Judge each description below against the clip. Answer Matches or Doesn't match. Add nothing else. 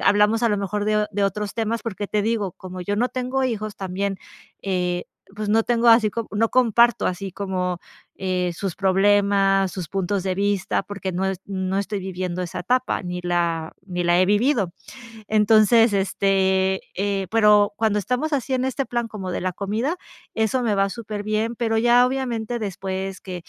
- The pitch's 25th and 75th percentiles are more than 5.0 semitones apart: Doesn't match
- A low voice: Doesn't match